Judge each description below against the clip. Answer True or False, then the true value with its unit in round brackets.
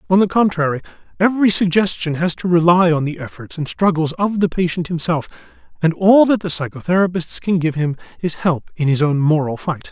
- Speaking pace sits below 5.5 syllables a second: False (5.6 syllables/s)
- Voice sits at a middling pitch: True (170 Hz)